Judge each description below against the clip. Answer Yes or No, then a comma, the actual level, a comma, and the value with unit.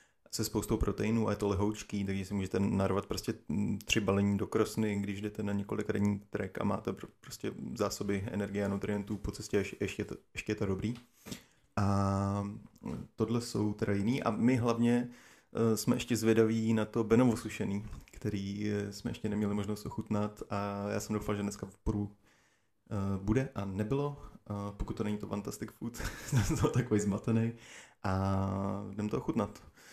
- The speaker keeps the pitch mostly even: Yes, narrow, 1.8 semitones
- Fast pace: Yes, fast, 175 wpm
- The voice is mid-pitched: No, low, 105 Hz